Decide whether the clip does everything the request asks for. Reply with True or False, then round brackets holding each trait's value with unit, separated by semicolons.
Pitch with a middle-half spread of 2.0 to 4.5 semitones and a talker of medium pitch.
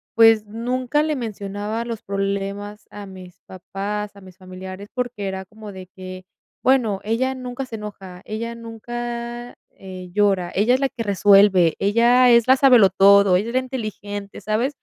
False (3.5 semitones; 210 Hz)